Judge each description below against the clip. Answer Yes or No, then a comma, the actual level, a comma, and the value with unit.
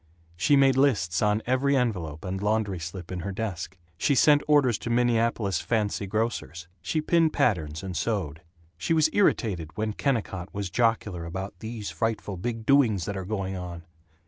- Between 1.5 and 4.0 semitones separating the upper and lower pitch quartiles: No, average, 4.8 semitones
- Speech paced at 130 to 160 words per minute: No, average, 170 wpm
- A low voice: Yes, low, 105 Hz